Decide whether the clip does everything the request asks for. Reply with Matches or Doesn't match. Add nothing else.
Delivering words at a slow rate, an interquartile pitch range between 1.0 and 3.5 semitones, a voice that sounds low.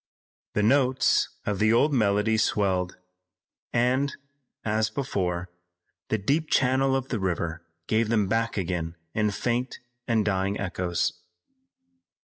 Doesn't match